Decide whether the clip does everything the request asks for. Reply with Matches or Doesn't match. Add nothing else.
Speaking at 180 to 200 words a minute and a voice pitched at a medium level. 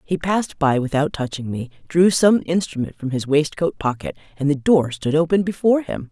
Matches